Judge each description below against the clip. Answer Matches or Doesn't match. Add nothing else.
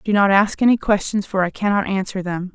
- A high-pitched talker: Matches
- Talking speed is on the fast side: Matches